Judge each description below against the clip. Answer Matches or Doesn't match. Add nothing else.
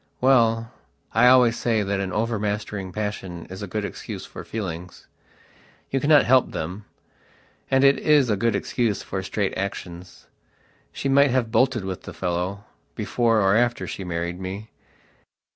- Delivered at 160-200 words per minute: Doesn't match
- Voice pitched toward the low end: Matches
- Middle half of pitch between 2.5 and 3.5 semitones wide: Doesn't match